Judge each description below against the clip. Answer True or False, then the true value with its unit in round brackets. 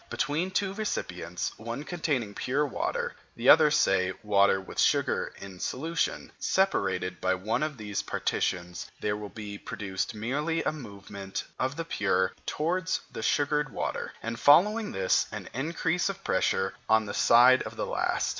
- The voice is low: True (120 Hz)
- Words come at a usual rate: True (155 wpm)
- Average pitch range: False (8.4 semitones)